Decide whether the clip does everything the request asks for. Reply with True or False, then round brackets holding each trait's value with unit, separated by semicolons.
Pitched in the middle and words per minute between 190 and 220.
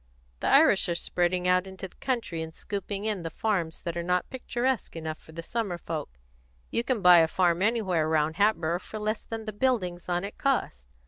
True (180 Hz; 205 wpm)